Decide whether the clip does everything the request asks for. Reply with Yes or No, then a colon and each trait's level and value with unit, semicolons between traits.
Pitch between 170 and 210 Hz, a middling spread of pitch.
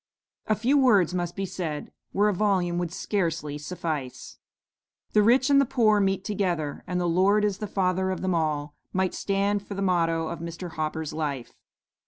Yes: medium, 185 Hz; average, 3.7 semitones